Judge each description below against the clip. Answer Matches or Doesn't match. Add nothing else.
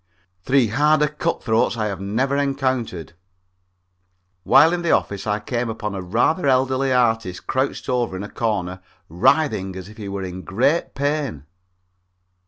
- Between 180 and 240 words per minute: Doesn't match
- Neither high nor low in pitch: Doesn't match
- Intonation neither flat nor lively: Doesn't match